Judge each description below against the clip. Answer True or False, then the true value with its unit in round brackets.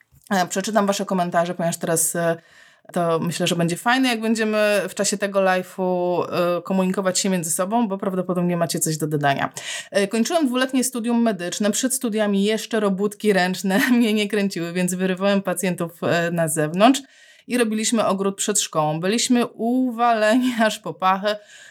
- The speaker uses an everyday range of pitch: True (4.1 semitones)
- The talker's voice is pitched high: True (200 Hz)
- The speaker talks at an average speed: True (145 wpm)